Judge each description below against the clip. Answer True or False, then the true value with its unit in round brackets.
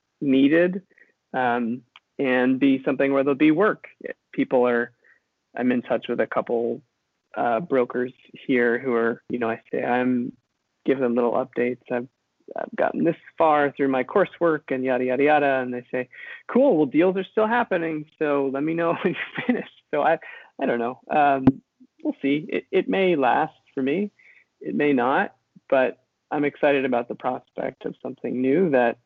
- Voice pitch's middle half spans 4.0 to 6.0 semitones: False (3.6 semitones)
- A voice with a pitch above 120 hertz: True (135 Hz)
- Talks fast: False (180 wpm)